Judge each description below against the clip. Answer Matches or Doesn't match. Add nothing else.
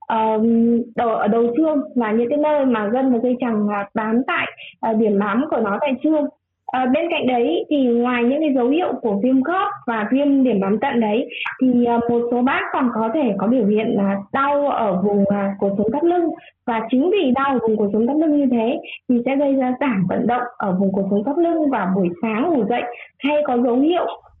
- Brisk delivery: Doesn't match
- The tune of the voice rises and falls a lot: Doesn't match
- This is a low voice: Doesn't match